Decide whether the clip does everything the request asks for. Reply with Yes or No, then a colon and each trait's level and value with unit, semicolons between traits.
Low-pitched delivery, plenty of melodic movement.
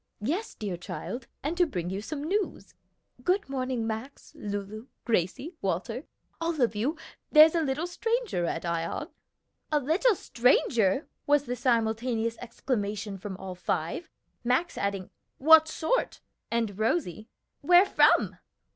No: high, 245 Hz; wide, 7.3 semitones